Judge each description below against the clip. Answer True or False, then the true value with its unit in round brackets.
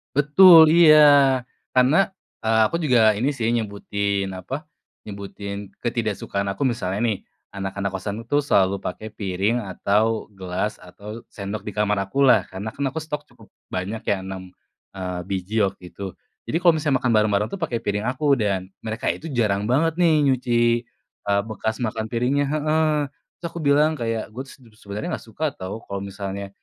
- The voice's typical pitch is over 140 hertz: False (110 Hz)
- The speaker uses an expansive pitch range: True (5.7 semitones)